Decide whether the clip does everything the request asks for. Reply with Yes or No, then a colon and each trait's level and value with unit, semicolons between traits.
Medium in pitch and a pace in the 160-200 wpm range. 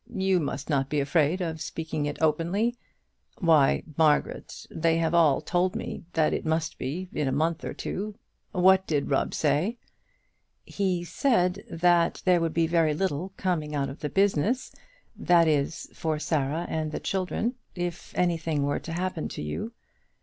Yes: medium, 165 Hz; average, 170 wpm